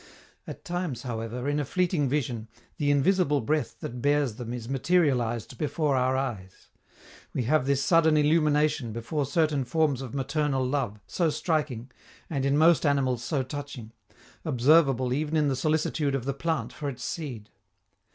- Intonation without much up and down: No, average, 3.5 semitones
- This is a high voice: No, medium, 140 Hz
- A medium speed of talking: Yes, average, 160 wpm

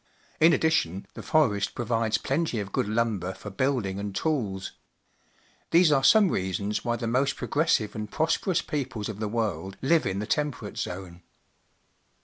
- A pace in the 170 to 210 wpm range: No, average, 155 wpm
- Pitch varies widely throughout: Yes, wide, 6.2 semitones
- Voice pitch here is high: No, low, 110 Hz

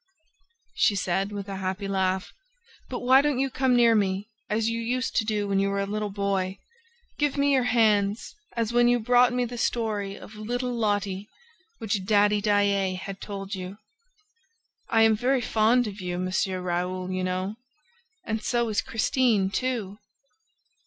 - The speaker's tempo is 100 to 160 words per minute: No, average, 170 wpm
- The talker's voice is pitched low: No, high, 210 Hz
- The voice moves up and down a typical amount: Yes, average, 3.4 semitones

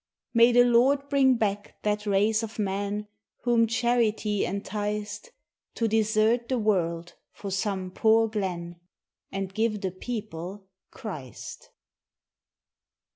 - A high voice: Yes, high, 210 Hz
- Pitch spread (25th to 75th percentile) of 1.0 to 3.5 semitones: Yes, average, 2.8 semitones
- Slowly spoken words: Yes, slow, 115 wpm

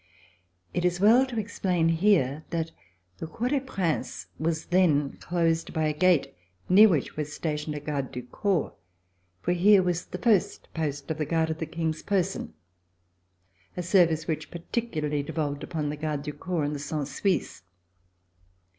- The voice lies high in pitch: No, medium, 165 Hz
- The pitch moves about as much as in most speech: Yes, average, 3.4 semitones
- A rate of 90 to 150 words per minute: No, average, 165 wpm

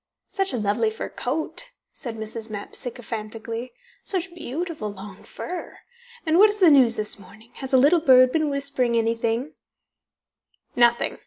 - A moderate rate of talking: Yes, average, 145 wpm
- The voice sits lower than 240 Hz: No, high, 245 Hz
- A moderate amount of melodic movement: No, wide, 5.9 semitones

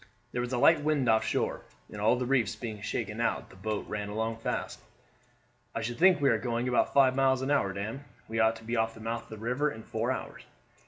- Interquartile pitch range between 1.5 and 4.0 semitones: Yes, average, 2.8 semitones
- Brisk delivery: Yes, fast, 245 wpm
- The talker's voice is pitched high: No, low, 115 Hz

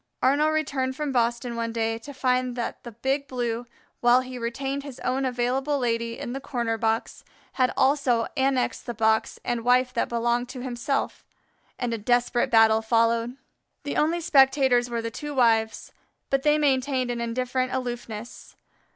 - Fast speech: No, average, 165 wpm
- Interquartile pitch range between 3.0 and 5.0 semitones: No, narrow, 2.4 semitones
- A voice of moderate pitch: No, high, 245 Hz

